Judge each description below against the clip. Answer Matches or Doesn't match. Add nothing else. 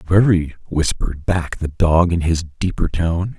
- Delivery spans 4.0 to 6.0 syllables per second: Matches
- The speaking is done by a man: Matches